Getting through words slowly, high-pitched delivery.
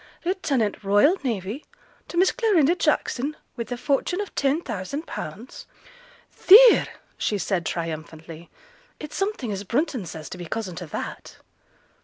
Yes: slow, 130 wpm; high, 240 Hz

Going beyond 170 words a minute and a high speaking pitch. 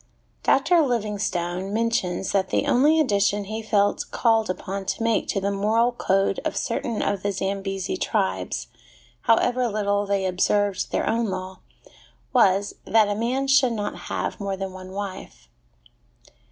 No: average, 150 wpm; high, 205 Hz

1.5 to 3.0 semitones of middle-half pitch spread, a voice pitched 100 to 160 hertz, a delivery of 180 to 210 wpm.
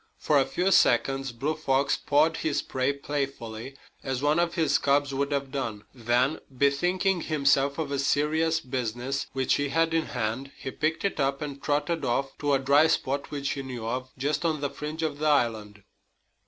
Yes: narrow, 2.4 semitones; medium, 140 Hz; average, 190 wpm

